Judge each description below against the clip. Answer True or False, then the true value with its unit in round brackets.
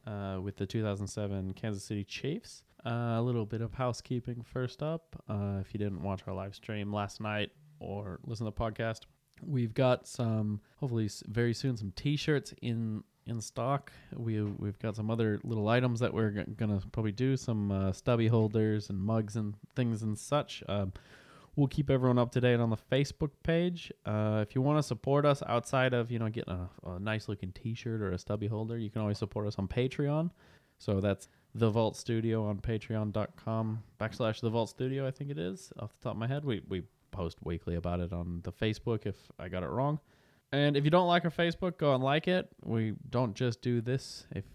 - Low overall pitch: True (115 Hz)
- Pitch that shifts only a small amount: False (3.8 semitones)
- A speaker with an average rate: False (210 wpm)